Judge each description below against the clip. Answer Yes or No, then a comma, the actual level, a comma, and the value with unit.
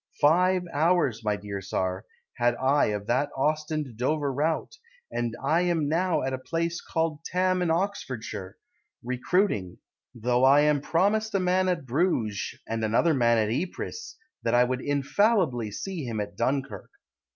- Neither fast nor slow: Yes, average, 150 wpm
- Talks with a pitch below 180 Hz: Yes, medium, 140 Hz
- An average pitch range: No, wide, 6.5 semitones